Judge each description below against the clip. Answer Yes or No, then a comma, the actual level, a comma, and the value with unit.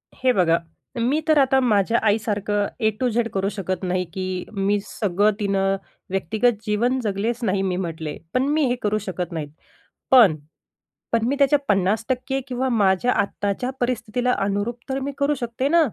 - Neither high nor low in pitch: No, high, 215 Hz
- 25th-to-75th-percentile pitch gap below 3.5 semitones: No, average, 4.4 semitones